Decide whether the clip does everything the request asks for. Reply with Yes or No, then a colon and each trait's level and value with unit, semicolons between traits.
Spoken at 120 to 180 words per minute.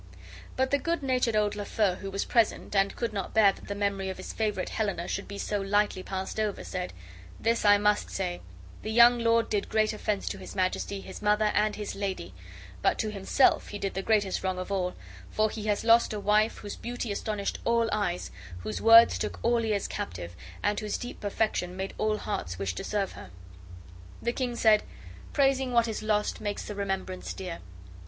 No: average, 200 wpm